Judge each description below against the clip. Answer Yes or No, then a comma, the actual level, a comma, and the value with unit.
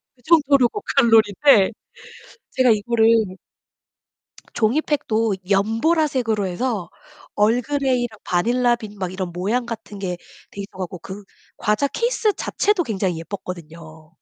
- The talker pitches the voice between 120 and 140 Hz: No, high, 220 Hz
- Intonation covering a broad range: No, average, 5.0 semitones